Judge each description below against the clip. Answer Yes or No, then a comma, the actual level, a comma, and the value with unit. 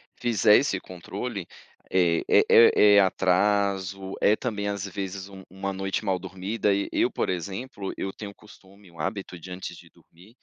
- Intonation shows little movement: Yes, narrow, 1.6 semitones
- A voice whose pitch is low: Yes, very low, 95 Hz